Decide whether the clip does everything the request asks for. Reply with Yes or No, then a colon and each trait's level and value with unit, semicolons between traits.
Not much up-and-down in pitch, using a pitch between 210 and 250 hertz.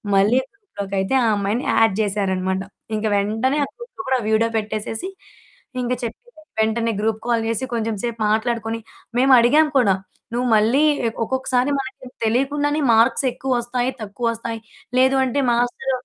No: average, 3.1 semitones; high, 235 Hz